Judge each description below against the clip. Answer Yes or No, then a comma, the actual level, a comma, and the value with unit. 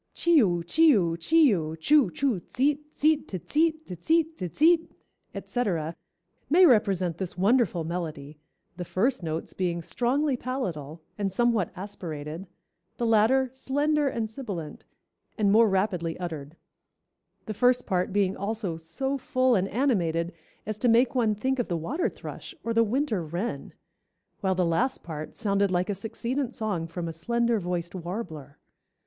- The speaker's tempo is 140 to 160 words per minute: Yes, average, 155 wpm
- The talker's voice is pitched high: Yes, high, 205 Hz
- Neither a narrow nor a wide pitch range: No, wide, 6.8 semitones